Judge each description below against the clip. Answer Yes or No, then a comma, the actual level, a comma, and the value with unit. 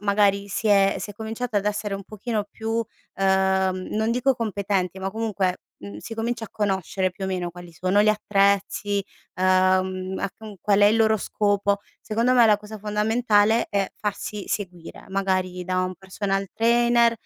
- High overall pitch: Yes, high, 200 Hz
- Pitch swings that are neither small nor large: No, narrow, 2.3 semitones